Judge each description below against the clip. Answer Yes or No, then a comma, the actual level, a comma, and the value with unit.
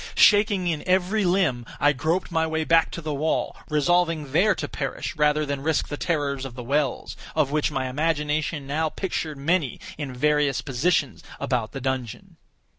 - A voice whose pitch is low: No, medium, 150 Hz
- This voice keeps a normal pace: Yes, average, 170 wpm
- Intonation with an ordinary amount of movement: Yes, average, 3.1 semitones